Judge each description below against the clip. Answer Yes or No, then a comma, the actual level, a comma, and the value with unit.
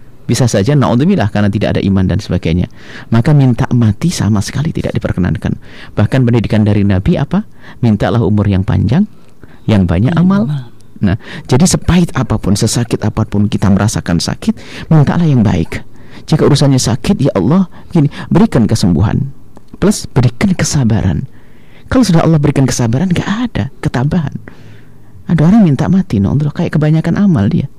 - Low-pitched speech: Yes, low, 125 Hz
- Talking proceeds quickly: Yes, fast, 150 wpm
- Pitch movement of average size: No, wide, 7.2 semitones